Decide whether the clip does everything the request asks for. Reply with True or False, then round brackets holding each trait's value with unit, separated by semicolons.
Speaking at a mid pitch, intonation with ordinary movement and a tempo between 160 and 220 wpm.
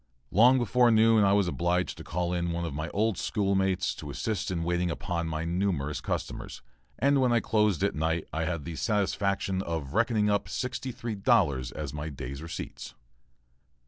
False (90 Hz; 4.6 semitones; 180 wpm)